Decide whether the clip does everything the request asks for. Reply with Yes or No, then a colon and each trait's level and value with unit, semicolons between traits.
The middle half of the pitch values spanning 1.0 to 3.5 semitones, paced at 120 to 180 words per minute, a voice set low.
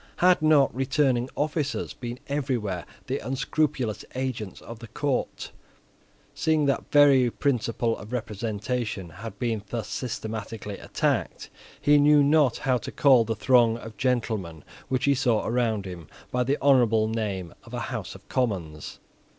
No: average, 3.9 semitones; average, 150 wpm; low, 120 Hz